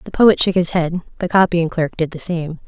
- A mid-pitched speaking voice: Yes, medium, 170 Hz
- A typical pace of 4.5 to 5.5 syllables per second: Yes, 5.2 syllables/s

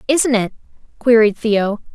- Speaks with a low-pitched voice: No, high, 225 Hz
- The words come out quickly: No, slow, 125 wpm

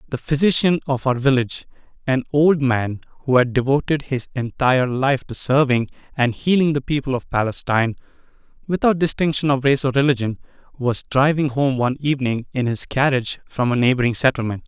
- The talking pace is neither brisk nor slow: Yes, average, 165 wpm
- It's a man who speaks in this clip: Yes, male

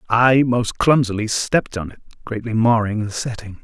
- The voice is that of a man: Yes, male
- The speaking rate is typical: Yes, average, 165 wpm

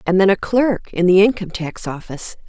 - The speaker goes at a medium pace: No, fast, 220 wpm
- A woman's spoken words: Yes, female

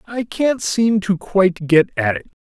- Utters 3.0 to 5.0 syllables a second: Yes, 4.1 syllables/s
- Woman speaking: No, male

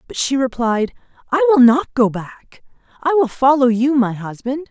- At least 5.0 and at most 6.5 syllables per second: No, 4.5 syllables/s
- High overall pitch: Yes, very high, 255 Hz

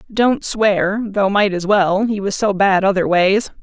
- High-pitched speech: Yes, high, 200 Hz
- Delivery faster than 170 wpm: Yes, average, 200 wpm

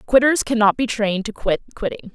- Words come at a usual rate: Yes, average, 195 wpm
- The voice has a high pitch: Yes, high, 230 Hz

